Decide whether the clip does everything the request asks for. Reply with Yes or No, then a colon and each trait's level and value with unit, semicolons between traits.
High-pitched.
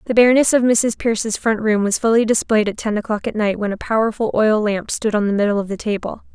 Yes: high, 215 Hz